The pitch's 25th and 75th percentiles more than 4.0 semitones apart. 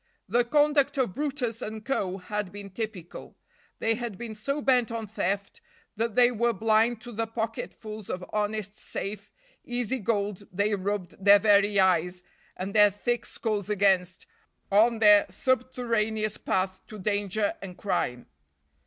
No: average, 2.8 semitones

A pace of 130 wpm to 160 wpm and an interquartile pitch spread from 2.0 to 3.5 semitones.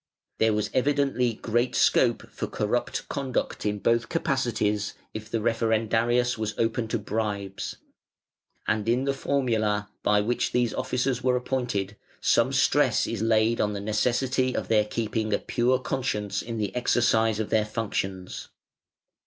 Yes: average, 145 wpm; narrow, 2.6 semitones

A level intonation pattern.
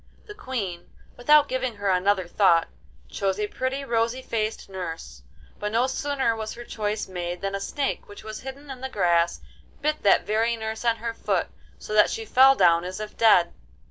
No: average, 5.0 semitones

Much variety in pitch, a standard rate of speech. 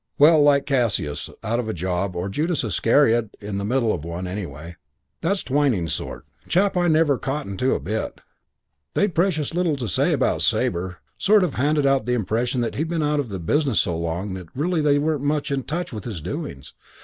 No: wide, 7.6 semitones; fast, 210 wpm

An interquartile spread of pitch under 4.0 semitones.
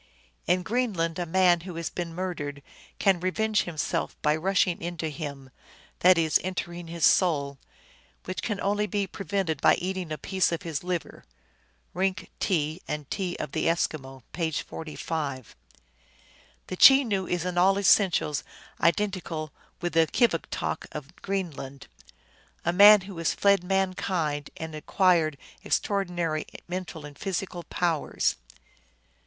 Yes: average, 3.3 semitones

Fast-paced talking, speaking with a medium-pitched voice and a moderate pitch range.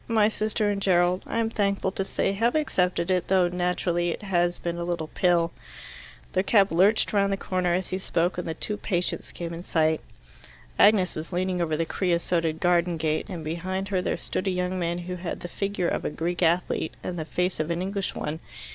No: fast, 215 wpm; medium, 180 Hz; narrow, 2.1 semitones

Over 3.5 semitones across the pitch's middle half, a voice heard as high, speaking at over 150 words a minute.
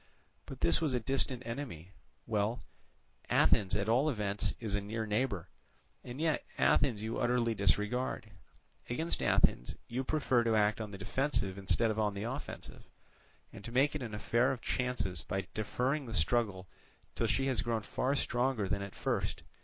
No: average, 3.9 semitones; low, 115 Hz; average, 170 wpm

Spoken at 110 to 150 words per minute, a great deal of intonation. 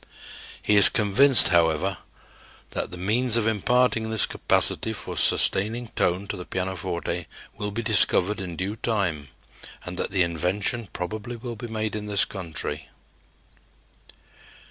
No: average, 140 wpm; average, 3.7 semitones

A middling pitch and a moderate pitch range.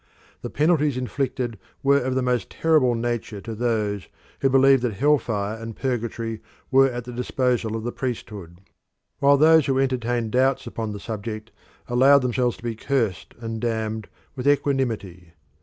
No: low, 120 Hz; average, 3.1 semitones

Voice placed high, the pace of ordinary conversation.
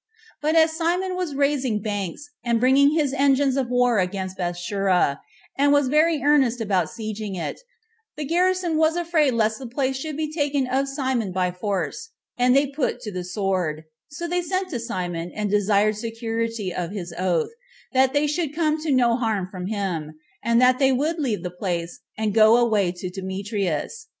Yes: high, 235 Hz; average, 190 wpm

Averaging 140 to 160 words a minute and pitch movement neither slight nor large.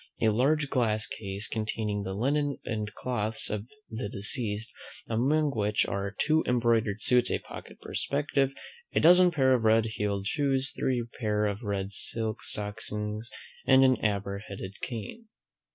Yes: average, 150 wpm; average, 4.2 semitones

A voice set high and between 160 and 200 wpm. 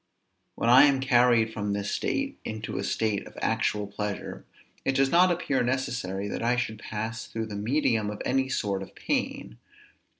No: low, 115 Hz; average, 175 wpm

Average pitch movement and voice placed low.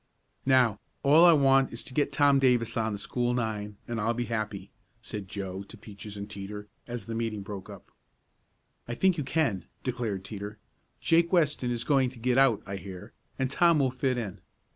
Yes: average, 4.5 semitones; low, 115 Hz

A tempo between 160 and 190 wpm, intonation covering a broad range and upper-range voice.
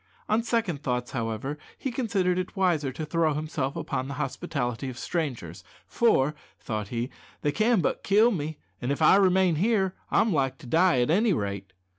No: average, 185 wpm; wide, 6.6 semitones; medium, 155 Hz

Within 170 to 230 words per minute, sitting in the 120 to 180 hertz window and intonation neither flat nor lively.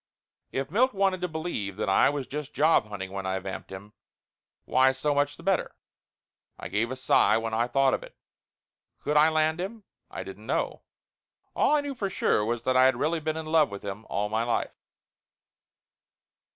No: average, 195 wpm; low, 135 Hz; wide, 6.6 semitones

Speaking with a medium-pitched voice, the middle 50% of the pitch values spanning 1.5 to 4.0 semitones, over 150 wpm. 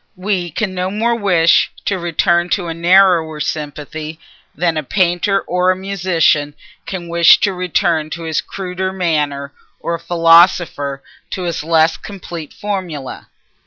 No: medium, 175 Hz; average, 2.8 semitones; average, 145 wpm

